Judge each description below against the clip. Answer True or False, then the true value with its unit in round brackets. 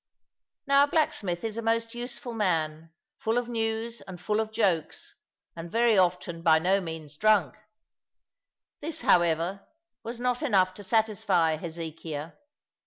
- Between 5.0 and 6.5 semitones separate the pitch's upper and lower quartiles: True (5.5 semitones)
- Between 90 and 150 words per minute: True (140 wpm)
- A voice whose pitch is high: True (200 Hz)